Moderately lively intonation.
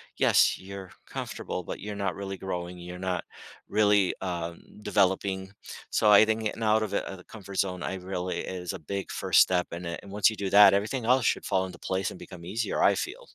No: narrow, 2.2 semitones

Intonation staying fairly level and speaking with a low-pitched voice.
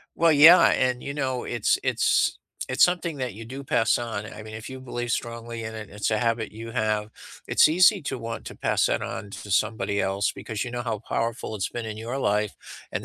No: average, 3.0 semitones; low, 115 Hz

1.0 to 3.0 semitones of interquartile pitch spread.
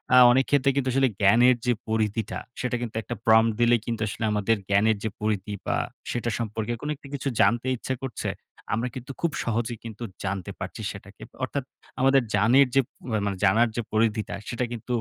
Yes: narrow, 2.6 semitones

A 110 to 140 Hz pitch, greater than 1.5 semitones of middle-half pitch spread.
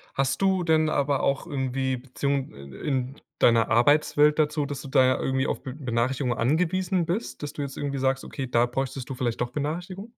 Yes: low, 135 Hz; average, 2.8 semitones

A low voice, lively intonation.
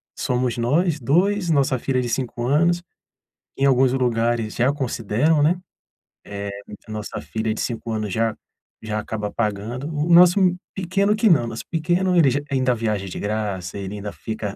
Yes: low, 125 Hz; wide, 6.2 semitones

